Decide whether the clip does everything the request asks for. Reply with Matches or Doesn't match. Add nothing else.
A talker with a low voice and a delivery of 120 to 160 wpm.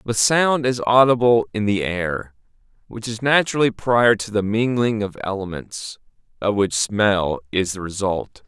Matches